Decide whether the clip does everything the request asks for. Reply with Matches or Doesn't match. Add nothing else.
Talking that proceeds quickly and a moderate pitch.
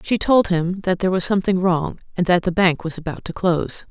Matches